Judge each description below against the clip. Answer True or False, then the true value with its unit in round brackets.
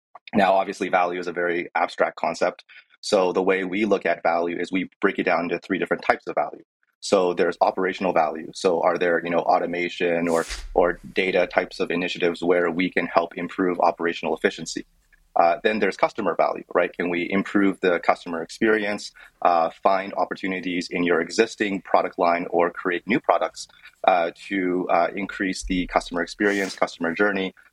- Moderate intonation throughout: False (2.0 semitones)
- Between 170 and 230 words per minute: True (175 wpm)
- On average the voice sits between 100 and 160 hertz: False (90 Hz)